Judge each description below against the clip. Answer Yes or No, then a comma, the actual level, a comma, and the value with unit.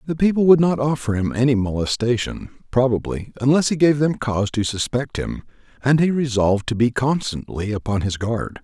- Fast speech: No, average, 180 wpm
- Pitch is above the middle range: No, low, 125 Hz